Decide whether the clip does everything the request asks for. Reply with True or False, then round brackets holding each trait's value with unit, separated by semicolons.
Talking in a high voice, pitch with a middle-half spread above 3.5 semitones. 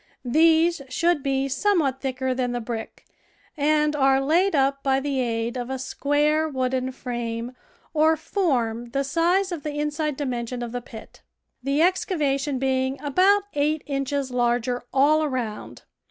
False (275 Hz; 3.2 semitones)